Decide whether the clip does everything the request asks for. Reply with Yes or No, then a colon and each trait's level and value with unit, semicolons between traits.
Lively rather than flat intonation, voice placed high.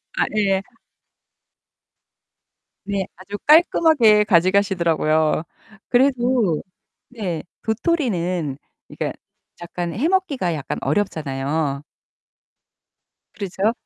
Yes: wide, 6.3 semitones; high, 195 Hz